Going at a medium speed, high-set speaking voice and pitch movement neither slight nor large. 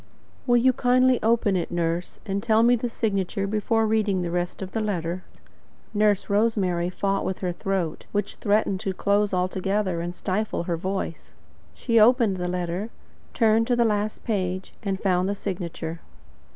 Yes: average, 165 wpm; high, 195 Hz; average, 3.3 semitones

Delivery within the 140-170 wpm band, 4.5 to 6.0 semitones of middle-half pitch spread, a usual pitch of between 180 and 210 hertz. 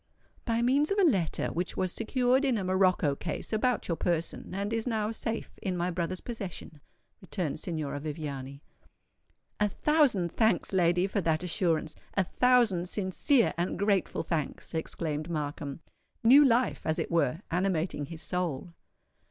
Yes: average, 150 wpm; wide, 5.4 semitones; medium, 185 Hz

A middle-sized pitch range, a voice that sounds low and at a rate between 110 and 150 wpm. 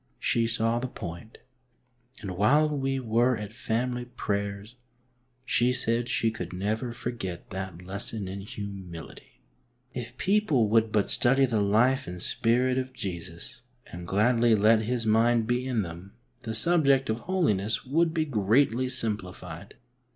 Yes: average, 4.0 semitones; low, 115 Hz; average, 145 wpm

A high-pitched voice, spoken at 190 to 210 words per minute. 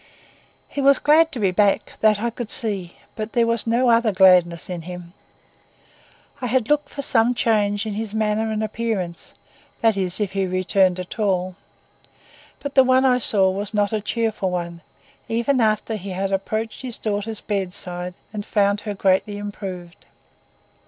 No: high, 210 Hz; average, 165 wpm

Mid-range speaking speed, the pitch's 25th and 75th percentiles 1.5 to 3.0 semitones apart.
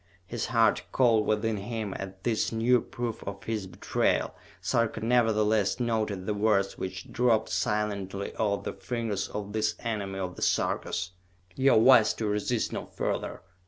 Yes: average, 160 wpm; narrow, 2.5 semitones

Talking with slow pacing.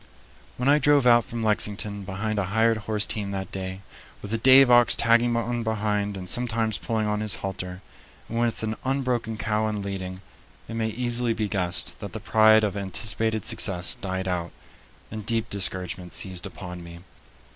No: average, 180 wpm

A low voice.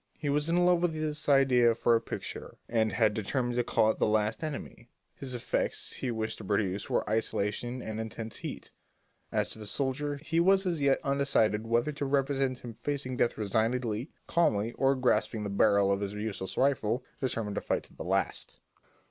Yes: low, 120 Hz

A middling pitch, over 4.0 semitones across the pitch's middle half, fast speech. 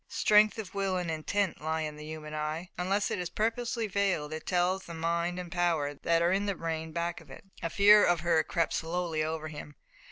No: medium, 170 Hz; average, 3.3 semitones; fast, 220 wpm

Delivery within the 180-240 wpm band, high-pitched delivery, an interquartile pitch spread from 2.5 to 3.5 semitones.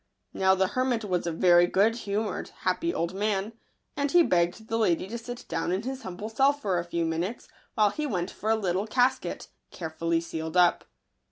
No: average, 195 wpm; high, 200 Hz; average, 4.8 semitones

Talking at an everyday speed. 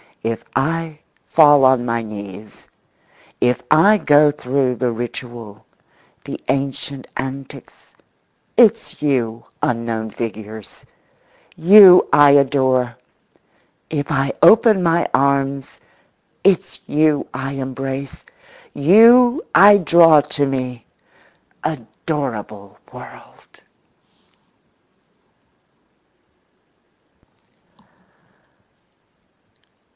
No: slow, 75 wpm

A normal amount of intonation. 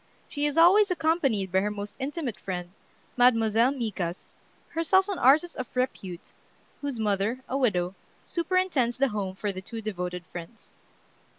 No: wide, 7.0 semitones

